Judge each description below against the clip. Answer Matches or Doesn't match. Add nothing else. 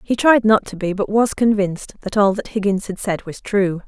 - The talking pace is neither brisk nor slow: Doesn't match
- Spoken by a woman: Matches